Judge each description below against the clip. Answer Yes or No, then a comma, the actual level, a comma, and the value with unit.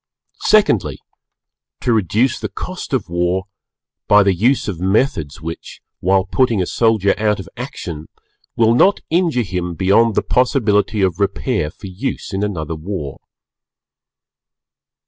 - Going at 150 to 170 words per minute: No, slow, 135 wpm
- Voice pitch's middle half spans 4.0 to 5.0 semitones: Yes, average, 4.7 semitones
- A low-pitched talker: Yes, low, 100 Hz